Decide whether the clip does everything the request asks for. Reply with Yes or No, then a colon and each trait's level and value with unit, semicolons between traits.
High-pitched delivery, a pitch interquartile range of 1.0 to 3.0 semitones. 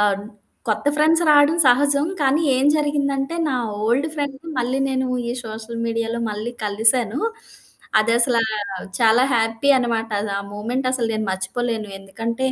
No: high, 240 Hz; average, 3.6 semitones